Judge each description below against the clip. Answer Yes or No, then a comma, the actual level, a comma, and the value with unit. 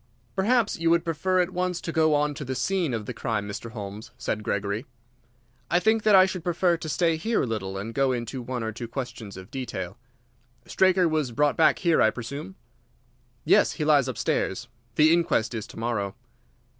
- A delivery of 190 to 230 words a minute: Yes, average, 195 wpm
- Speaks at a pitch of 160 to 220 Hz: No, medium, 140 Hz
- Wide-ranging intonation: Yes, wide, 7.1 semitones